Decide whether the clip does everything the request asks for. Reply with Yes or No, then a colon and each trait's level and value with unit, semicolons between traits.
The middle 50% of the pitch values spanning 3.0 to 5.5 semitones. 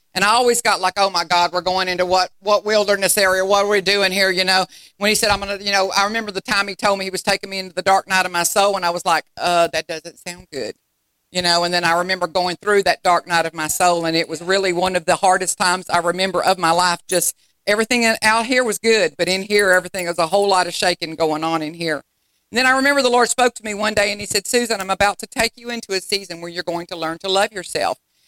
No: narrow, 2.6 semitones